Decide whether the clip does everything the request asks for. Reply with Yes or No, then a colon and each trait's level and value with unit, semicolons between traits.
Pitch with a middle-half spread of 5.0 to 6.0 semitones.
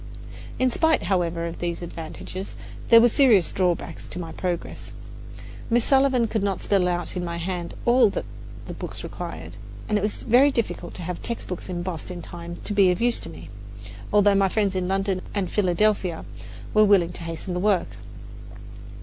No: average, 3.5 semitones